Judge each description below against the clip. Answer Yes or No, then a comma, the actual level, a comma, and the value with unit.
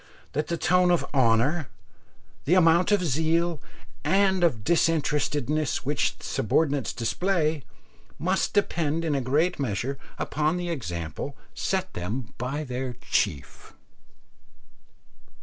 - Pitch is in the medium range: Yes, medium, 150 Hz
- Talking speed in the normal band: No, slow, 115 wpm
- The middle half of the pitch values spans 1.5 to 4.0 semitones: No, average, 4.8 semitones